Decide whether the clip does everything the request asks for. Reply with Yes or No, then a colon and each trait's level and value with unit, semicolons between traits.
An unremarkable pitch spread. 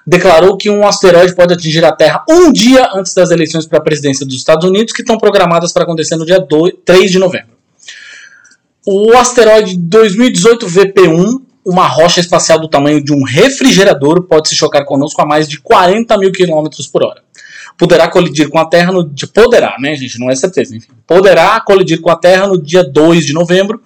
Yes: average, 4.0 semitones